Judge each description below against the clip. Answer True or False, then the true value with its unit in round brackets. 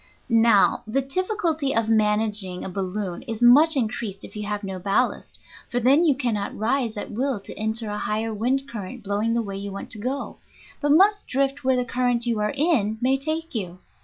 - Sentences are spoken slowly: False (200 wpm)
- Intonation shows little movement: False (4.5 semitones)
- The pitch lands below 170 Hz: False (230 Hz)